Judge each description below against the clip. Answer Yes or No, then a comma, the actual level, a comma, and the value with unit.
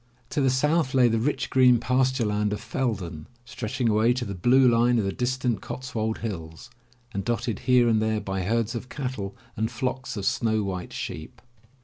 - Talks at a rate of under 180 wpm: No, average, 190 wpm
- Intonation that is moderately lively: Yes, average, 3.3 semitones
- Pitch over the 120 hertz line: No, low, 115 Hz